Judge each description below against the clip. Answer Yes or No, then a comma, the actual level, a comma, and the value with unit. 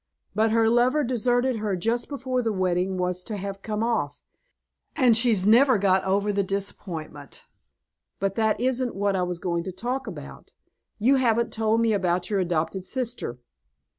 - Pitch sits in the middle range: No, high, 210 Hz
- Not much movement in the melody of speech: No, average, 4.3 semitones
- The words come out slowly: No, average, 165 wpm